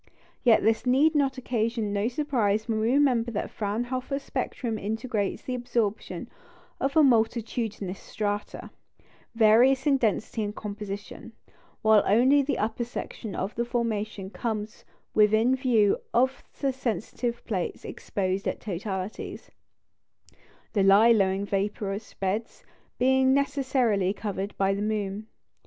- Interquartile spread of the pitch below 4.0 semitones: Yes, average, 3.6 semitones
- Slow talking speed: Yes, slow, 125 wpm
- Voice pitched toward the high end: Yes, high, 220 Hz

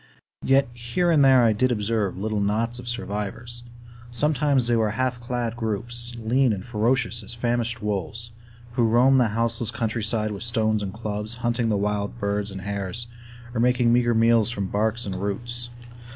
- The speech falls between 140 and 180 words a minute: Yes, average, 170 wpm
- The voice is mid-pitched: No, low, 115 Hz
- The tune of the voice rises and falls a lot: No, narrow, 2.4 semitones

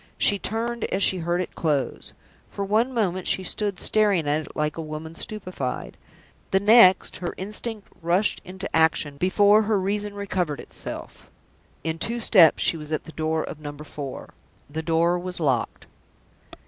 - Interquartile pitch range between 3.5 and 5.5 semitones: Yes, average, 4.4 semitones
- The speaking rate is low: No, average, 165 wpm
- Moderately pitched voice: Yes, medium, 180 Hz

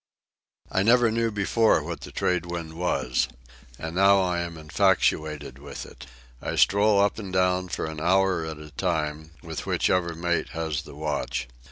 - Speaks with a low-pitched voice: Yes, very low, 85 Hz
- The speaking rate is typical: Yes, average, 170 wpm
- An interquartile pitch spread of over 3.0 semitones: Yes, average, 3.6 semitones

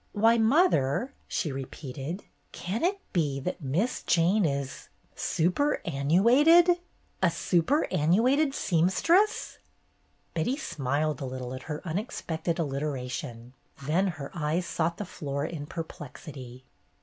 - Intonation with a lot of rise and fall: Yes, wide, 7.6 semitones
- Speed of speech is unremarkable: No, slow, 125 wpm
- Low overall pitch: No, medium, 165 Hz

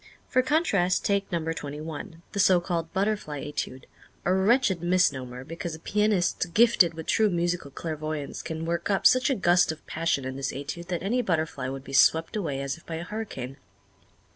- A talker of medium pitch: Yes, medium, 170 Hz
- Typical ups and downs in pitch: Yes, average, 4.5 semitones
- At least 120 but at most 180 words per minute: No, average, 190 wpm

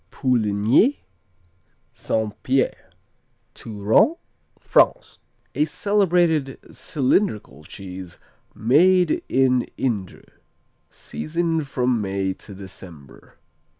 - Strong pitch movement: Yes, wide, 7.9 semitones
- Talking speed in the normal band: No, slow, 75 wpm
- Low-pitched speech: Yes, low, 125 Hz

